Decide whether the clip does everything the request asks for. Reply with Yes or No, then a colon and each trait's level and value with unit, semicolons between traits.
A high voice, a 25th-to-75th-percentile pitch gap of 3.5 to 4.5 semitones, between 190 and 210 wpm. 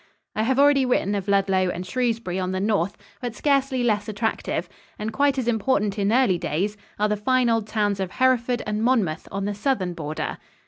Yes: high, 210 Hz; average, 4.1 semitones; average, 195 wpm